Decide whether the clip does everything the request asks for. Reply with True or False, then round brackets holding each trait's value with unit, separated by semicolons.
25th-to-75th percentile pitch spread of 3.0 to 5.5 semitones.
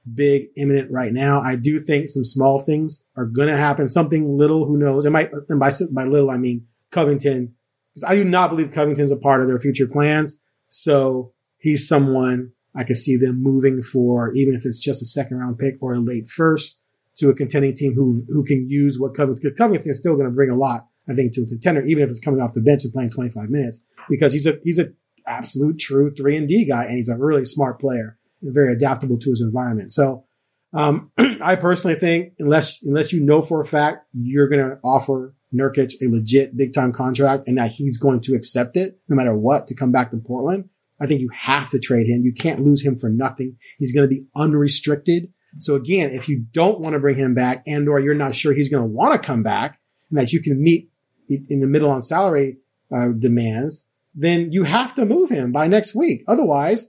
False (2.6 semitones)